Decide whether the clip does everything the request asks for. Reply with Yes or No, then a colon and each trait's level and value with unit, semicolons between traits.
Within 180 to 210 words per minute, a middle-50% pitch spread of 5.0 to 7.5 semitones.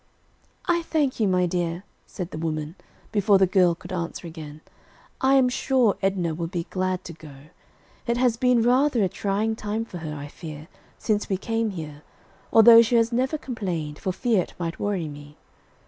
Yes: average, 185 wpm; wide, 5.5 semitones